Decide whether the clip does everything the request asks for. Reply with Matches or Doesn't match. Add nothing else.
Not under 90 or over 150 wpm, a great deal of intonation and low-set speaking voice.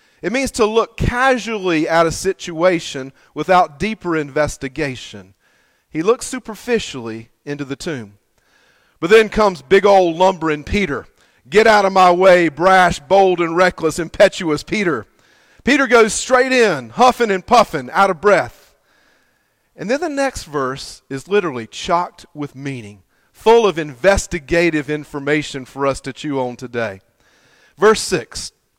Doesn't match